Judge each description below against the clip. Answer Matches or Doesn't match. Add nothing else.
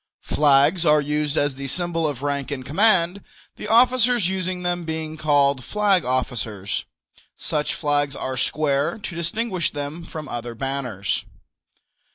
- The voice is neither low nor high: Matches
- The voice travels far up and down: Doesn't match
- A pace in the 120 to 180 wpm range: Matches